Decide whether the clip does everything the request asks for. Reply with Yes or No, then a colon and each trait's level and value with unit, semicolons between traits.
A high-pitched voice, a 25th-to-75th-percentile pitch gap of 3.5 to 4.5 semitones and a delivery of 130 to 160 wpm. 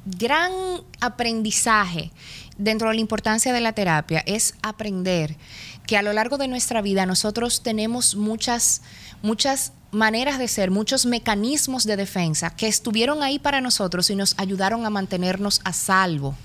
Yes: high, 215 Hz; average, 3.9 semitones; average, 150 wpm